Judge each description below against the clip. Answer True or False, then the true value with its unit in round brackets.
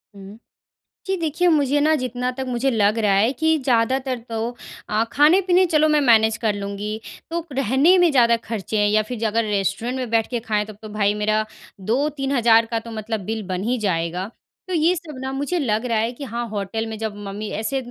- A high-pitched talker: True (230 Hz)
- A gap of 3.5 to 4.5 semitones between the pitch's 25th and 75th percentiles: True (4.2 semitones)